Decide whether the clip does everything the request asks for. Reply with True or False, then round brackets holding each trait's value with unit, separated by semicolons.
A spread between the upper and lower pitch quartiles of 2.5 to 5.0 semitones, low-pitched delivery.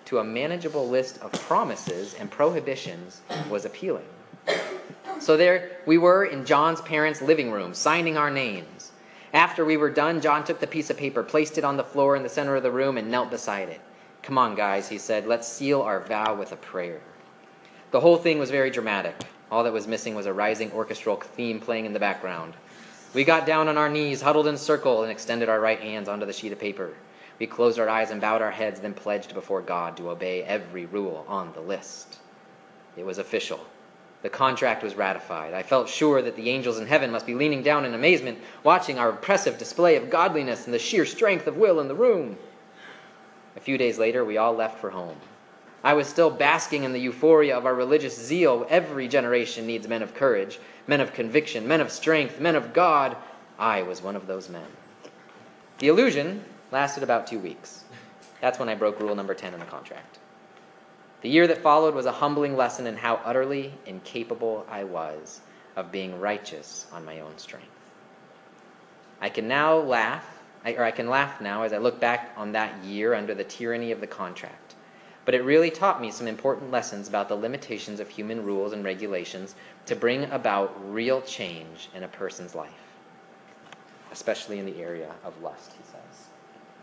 False (5.6 semitones; 120 Hz)